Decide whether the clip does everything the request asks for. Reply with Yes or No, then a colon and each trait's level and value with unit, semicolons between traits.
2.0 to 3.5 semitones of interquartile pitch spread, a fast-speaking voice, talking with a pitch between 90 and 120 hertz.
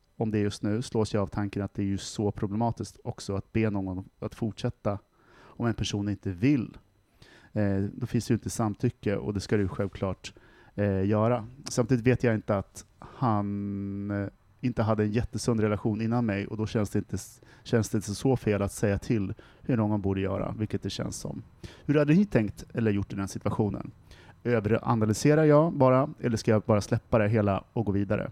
Yes: average, 2.8 semitones; fast, 200 wpm; low, 110 Hz